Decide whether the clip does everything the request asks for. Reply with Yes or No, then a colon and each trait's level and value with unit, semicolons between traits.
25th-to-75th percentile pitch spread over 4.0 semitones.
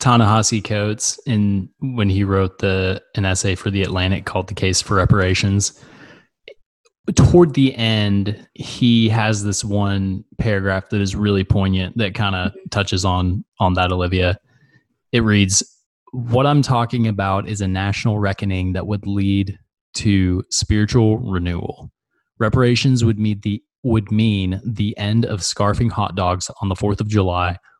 No: average, 2.8 semitones